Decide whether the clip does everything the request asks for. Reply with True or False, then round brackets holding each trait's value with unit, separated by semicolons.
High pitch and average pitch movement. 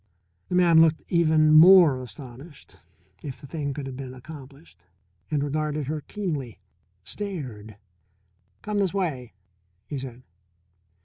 False (145 Hz; 4.0 semitones)